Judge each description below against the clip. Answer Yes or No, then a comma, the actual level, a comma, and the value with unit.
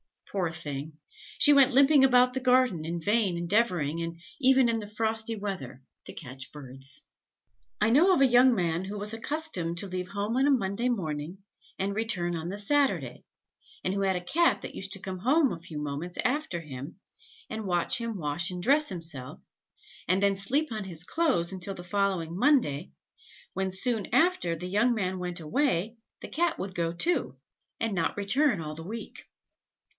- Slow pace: No, average, 180 wpm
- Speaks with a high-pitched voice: Yes, high, 195 Hz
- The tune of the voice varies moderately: No, wide, 6.2 semitones